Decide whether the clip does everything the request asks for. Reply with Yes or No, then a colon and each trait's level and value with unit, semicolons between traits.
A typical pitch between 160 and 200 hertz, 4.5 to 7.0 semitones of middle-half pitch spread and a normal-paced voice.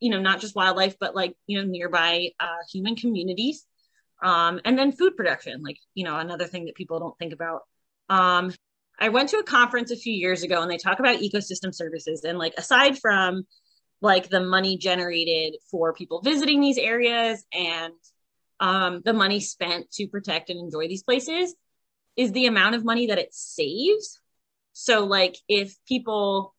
Yes: high, 190 Hz; average, 5.2 semitones; average, 180 wpm